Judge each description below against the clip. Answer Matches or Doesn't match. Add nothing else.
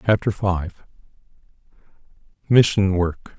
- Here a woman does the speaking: Doesn't match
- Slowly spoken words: Matches